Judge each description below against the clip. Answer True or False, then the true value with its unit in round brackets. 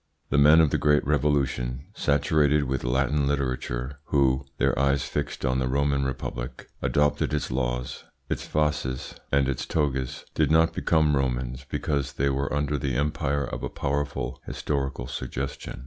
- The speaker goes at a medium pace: True (155 wpm)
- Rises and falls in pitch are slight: True (2.1 semitones)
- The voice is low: True (70 Hz)